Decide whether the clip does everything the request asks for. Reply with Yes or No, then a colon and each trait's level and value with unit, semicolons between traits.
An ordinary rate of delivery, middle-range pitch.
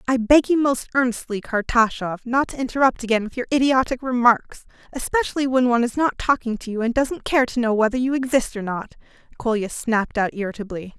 No: average, 195 wpm; high, 240 Hz